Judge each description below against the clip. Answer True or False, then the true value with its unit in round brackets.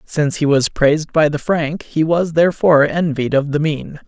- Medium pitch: True (155 Hz)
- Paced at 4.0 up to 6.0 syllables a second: True (5.1 syllables/s)